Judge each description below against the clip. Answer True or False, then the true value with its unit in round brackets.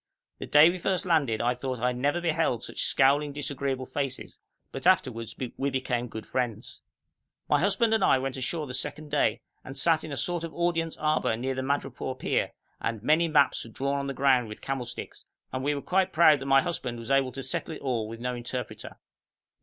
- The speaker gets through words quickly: True (215 wpm)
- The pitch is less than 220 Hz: True (135 Hz)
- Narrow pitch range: False (3.7 semitones)